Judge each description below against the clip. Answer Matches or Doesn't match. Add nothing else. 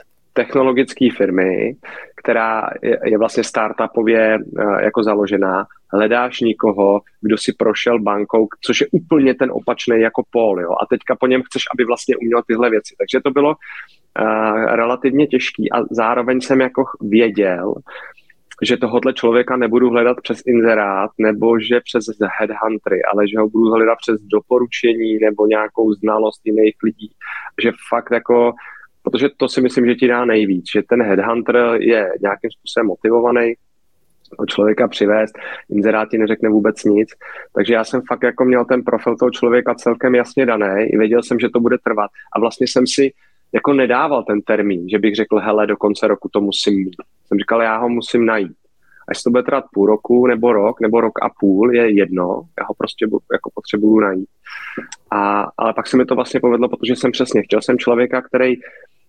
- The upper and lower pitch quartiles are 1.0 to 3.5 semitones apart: Matches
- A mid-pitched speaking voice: Doesn't match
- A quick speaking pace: Matches